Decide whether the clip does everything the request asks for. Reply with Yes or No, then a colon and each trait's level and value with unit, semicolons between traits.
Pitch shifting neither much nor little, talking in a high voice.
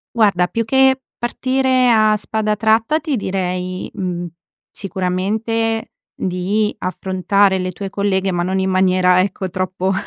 Yes: average, 3.3 semitones; high, 195 Hz